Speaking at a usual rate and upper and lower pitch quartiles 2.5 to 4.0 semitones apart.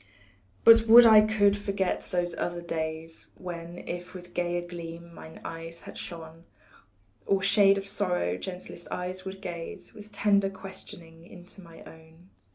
Yes: average, 150 wpm; average, 2.8 semitones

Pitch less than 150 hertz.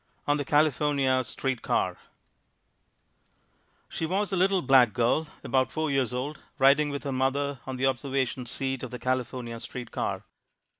Yes: low, 135 Hz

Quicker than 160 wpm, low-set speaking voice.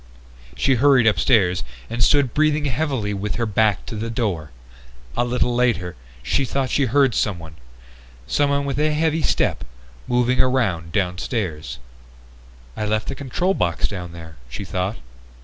No: average, 150 wpm; low, 115 Hz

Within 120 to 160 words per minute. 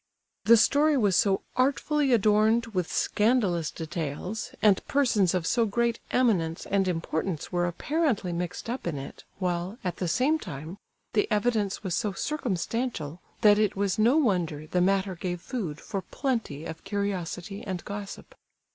Yes: average, 155 wpm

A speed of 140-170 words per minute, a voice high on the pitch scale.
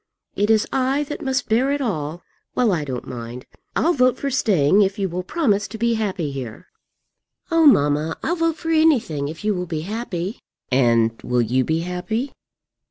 No: average, 185 wpm; high, 195 Hz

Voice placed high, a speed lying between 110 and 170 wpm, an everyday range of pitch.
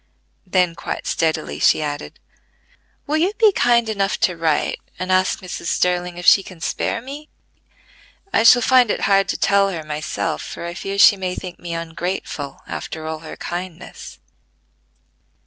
No: medium, 180 Hz; average, 165 wpm; average, 3.3 semitones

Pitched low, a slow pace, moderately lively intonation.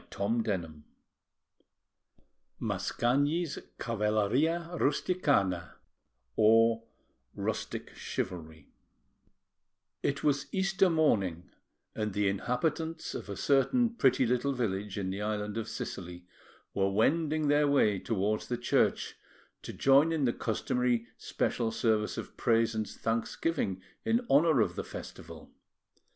No: low, 115 Hz; slow, 110 wpm; wide, 6.3 semitones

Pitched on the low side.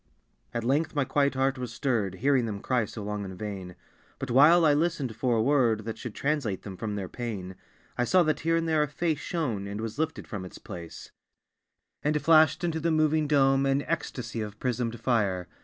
Yes: low, 125 Hz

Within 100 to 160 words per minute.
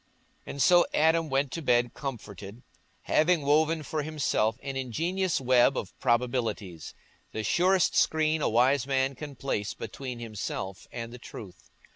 Yes: average, 140 wpm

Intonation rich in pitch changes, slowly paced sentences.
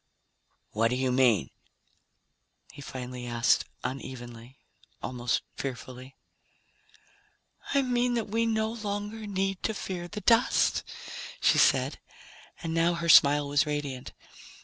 Yes: wide, 8.6 semitones; slow, 120 wpm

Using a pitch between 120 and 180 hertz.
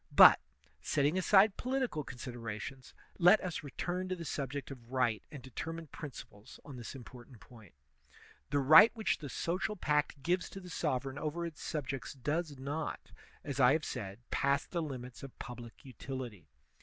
Yes: medium, 140 Hz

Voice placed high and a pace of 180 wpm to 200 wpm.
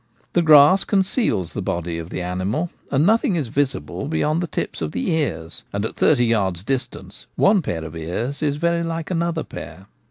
No: medium, 140 Hz; average, 190 wpm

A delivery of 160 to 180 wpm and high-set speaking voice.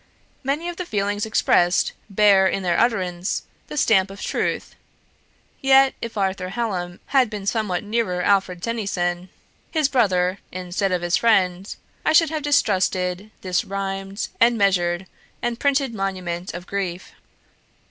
No: average, 140 wpm; high, 195 Hz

